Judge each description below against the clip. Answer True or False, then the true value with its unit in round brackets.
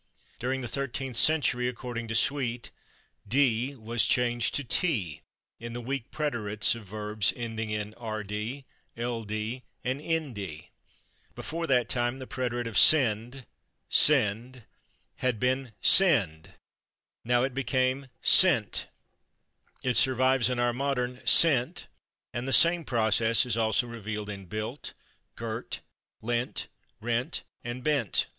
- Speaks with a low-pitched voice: True (120 Hz)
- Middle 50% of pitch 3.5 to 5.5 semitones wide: False (2.9 semitones)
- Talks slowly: True (125 wpm)